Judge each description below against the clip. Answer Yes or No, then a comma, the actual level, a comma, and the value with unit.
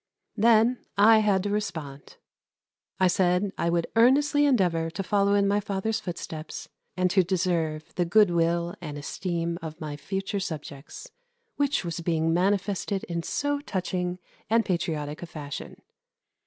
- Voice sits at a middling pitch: Yes, medium, 180 Hz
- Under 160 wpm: Yes, average, 145 wpm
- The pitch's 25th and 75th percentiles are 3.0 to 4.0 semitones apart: Yes, average, 3.7 semitones